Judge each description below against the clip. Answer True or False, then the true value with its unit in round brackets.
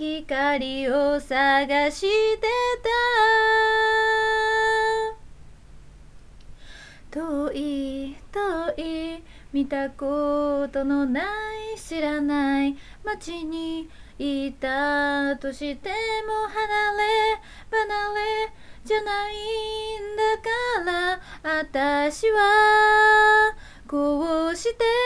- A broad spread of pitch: True (7.2 semitones)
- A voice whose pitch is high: True (370 Hz)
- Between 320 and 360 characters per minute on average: False (115 characters per minute)